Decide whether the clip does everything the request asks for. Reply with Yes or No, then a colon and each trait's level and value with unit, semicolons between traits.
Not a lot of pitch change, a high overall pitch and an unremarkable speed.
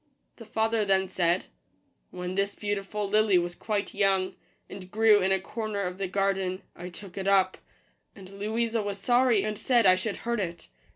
Yes: narrow, 2.3 semitones; high, 195 Hz; average, 185 wpm